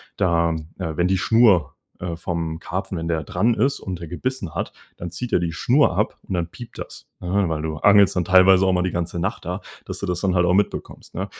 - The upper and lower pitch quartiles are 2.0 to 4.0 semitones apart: Yes, narrow, 2.4 semitones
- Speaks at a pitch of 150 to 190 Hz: No, very low, 90 Hz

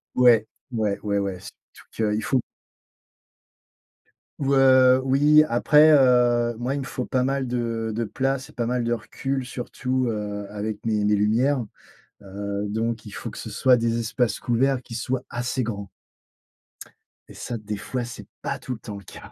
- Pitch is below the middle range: Yes, low, 120 Hz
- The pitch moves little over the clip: No, average, 3.3 semitones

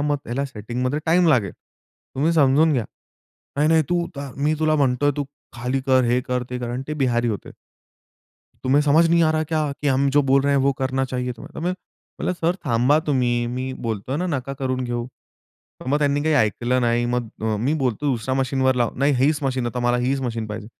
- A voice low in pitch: Yes, low, 130 Hz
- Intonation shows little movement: No, average, 3.0 semitones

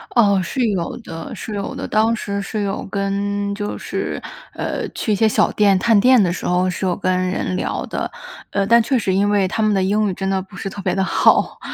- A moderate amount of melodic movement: No, narrow, 2.0 semitones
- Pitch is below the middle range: No, high, 200 Hz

